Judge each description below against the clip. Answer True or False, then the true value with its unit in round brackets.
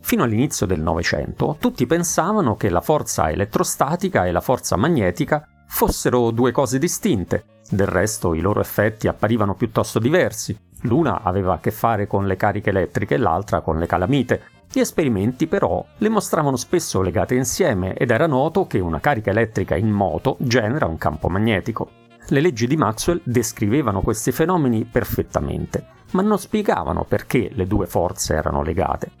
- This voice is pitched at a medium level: False (115 Hz)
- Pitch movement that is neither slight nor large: False (6.1 semitones)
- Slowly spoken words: False (160 wpm)